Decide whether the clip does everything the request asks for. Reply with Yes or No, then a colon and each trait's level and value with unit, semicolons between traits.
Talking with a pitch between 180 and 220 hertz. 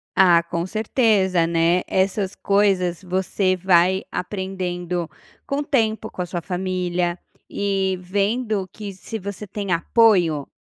Yes: high, 190 Hz